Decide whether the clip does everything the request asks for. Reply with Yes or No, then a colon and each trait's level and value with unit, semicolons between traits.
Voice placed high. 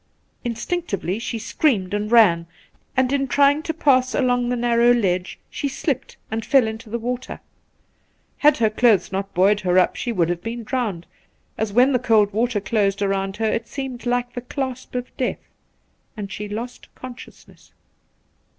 Yes: high, 235 Hz